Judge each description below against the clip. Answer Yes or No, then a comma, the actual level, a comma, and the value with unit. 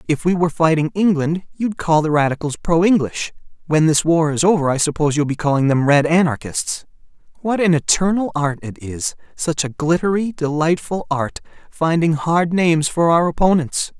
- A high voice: No, medium, 160 Hz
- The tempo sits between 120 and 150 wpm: No, average, 165 wpm